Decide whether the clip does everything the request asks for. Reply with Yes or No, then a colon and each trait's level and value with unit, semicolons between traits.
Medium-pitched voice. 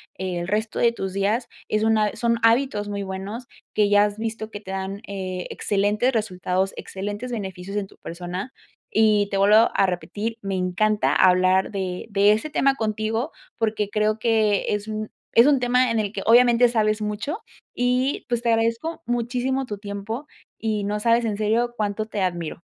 No: high, 215 Hz